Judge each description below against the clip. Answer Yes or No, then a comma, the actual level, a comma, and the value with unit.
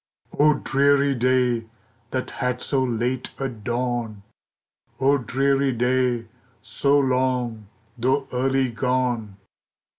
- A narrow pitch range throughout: Yes, narrow, 2.0 semitones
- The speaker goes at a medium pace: No, slow, 100 wpm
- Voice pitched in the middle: No, low, 125 Hz